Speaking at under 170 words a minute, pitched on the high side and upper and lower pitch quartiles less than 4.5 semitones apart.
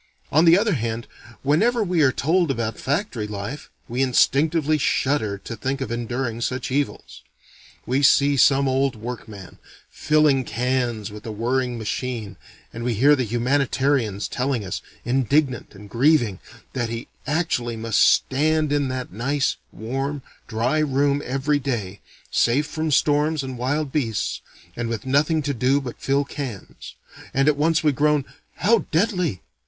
No: average, 155 wpm; low, 135 Hz; average, 3.8 semitones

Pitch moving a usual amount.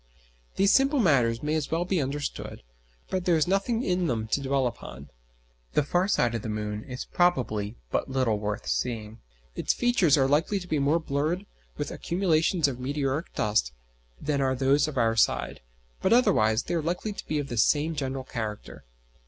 No: wide, 6.7 semitones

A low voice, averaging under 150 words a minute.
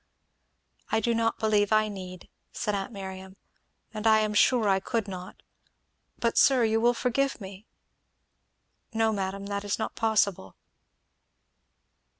No: high, 210 Hz; average, 140 wpm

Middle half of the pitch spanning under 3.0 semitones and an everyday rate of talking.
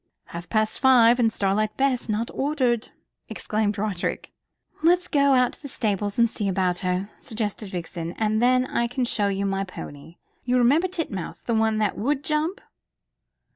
No: average, 4.3 semitones; average, 170 wpm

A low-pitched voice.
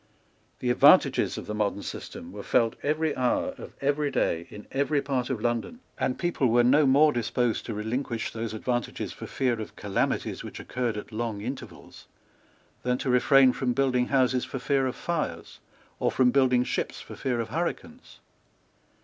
Yes: low, 125 Hz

